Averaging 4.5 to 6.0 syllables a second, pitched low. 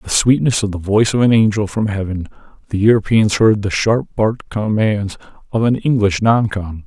Yes: 5.3 syllables/s; low, 105 Hz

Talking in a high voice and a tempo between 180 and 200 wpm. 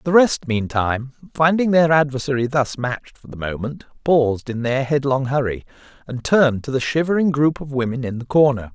No: low, 135 Hz; average, 185 wpm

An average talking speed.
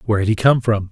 No: fast, 325 wpm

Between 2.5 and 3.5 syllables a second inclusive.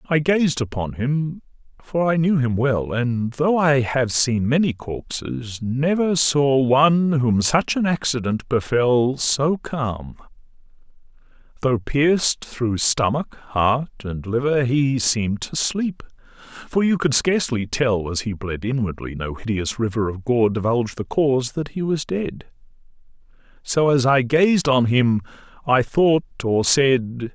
Yes: 3.2 syllables/s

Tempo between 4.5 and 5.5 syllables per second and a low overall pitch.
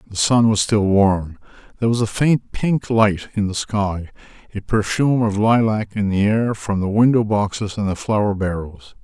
Yes: 4.6 syllables/s; low, 105 Hz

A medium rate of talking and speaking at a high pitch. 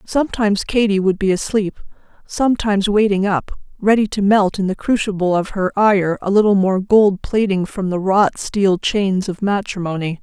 Yes: average, 170 wpm; high, 200 Hz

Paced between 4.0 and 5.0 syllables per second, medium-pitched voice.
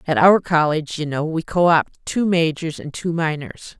Yes: 4.8 syllables/s; medium, 160 Hz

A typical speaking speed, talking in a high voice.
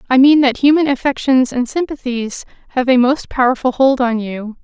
Yes: average, 180 wpm; very high, 260 Hz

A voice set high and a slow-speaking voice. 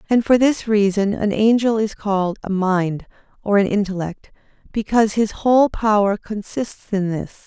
No: high, 210 Hz; average, 160 wpm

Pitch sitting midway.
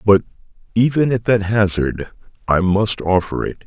No: low, 105 Hz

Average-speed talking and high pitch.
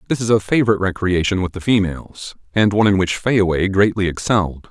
No: average, 190 wpm; low, 100 Hz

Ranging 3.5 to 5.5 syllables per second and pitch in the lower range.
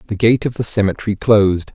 No: 6.5 syllables/s; low, 105 Hz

